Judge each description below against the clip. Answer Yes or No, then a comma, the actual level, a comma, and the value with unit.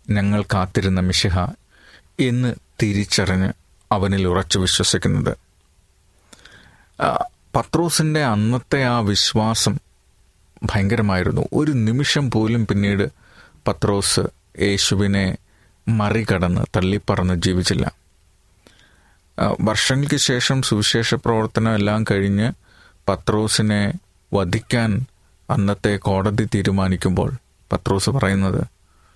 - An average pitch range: Yes, average, 3.2 semitones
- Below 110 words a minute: Yes, average, 70 wpm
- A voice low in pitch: Yes, low, 100 Hz